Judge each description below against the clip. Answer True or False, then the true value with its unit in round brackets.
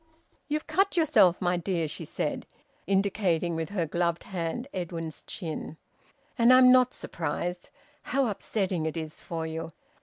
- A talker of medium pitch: True (180 Hz)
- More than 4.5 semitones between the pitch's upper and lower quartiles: True (5.1 semitones)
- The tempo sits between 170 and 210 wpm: False (145 wpm)